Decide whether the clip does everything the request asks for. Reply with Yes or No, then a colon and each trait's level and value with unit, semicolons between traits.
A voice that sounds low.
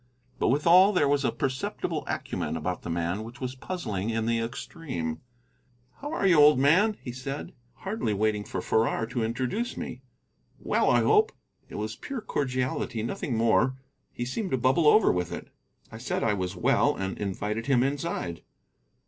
Yes: low, 125 Hz